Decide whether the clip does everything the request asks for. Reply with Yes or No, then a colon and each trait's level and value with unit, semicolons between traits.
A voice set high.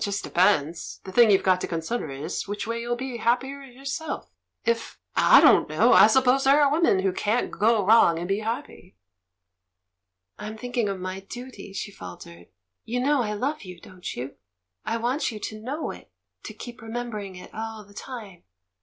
Yes: high, 220 Hz